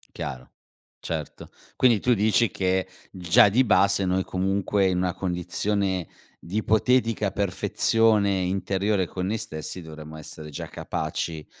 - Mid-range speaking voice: No, very low, 95 Hz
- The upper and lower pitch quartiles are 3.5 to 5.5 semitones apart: No, average, 2.7 semitones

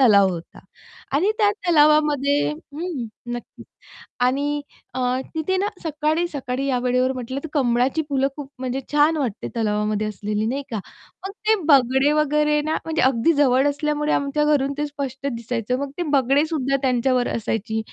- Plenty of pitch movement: No, average, 3.2 semitones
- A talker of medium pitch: No, very high, 275 Hz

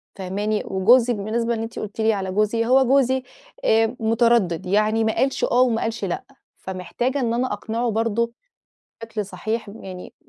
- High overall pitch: Yes, high, 225 Hz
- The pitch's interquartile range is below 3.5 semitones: Yes, narrow, 2.5 semitones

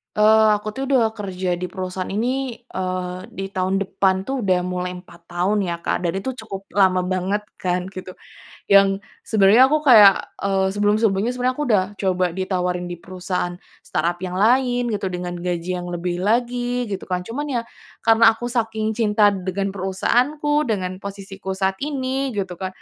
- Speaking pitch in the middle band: No, high, 195 Hz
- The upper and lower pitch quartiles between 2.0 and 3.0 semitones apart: No, average, 3.7 semitones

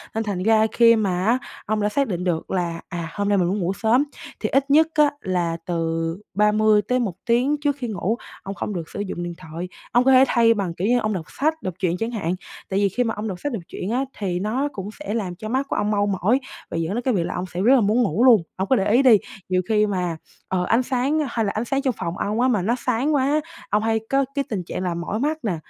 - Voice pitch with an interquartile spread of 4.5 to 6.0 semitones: Yes, average, 5.1 semitones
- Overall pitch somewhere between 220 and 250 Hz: No, high, 210 Hz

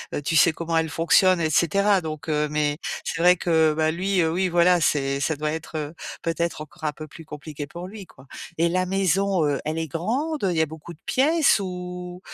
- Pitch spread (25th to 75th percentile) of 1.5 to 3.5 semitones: Yes, average, 2.8 semitones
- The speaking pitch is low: No, medium, 165 Hz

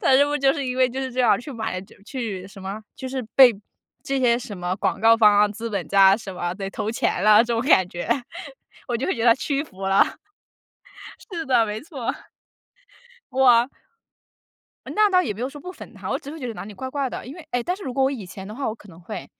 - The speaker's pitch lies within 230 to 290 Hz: Yes, high, 235 Hz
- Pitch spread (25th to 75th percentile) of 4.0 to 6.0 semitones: Yes, average, 4.5 semitones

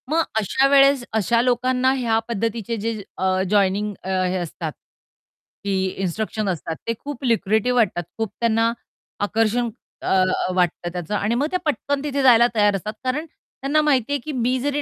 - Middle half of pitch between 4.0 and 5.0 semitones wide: Yes, average, 4.5 semitones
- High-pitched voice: Yes, high, 230 Hz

